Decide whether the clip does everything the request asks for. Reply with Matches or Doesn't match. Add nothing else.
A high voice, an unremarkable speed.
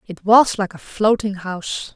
Matches